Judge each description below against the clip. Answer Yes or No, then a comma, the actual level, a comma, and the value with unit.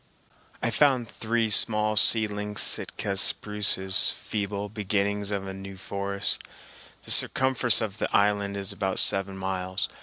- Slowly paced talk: Yes, slow, 130 wpm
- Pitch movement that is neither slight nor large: No, narrow, 1.7 semitones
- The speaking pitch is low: Yes, low, 100 Hz